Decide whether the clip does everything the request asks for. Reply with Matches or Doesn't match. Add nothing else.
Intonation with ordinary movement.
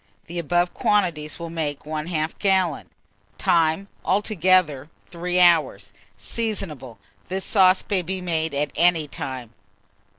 Matches